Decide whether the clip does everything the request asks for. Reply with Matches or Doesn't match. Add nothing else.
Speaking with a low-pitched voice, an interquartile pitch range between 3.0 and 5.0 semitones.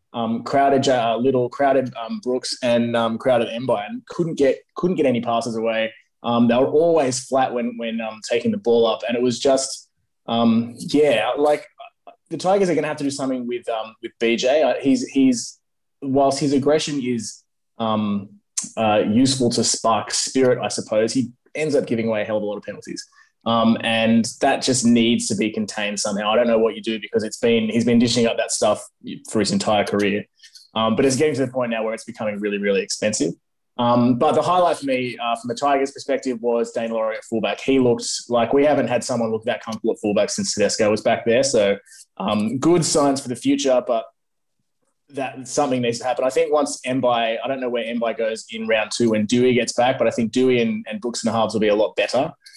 Matches